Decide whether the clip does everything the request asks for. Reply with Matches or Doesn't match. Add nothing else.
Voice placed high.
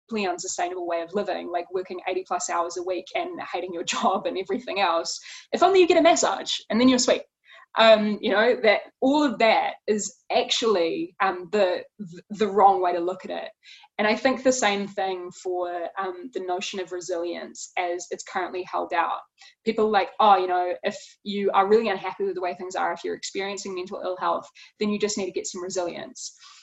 Matches